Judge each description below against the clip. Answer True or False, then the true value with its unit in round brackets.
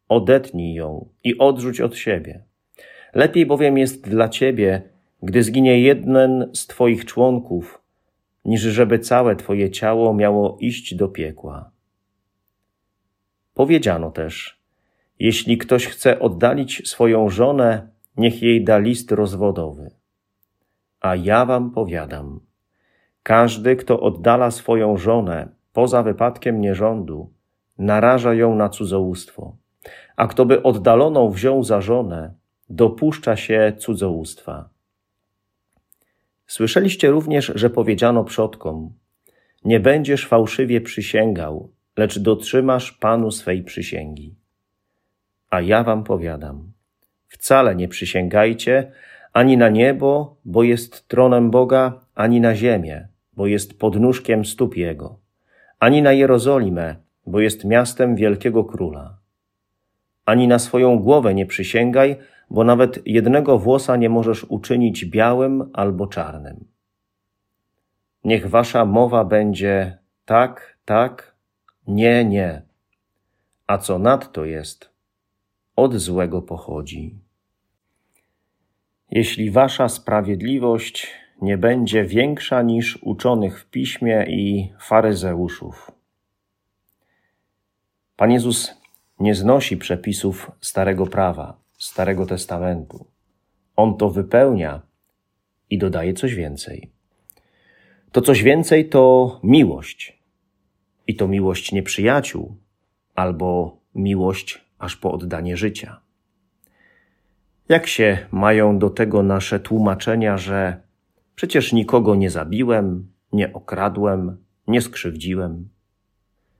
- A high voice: False (105 Hz)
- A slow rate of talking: True (100 wpm)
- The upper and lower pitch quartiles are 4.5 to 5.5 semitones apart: False (3.4 semitones)